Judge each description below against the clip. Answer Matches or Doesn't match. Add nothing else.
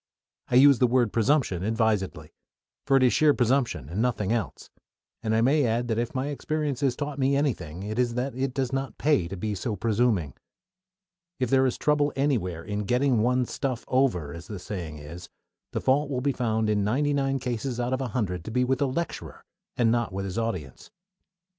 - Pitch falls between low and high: Doesn't match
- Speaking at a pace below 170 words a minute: Doesn't match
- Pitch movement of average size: Matches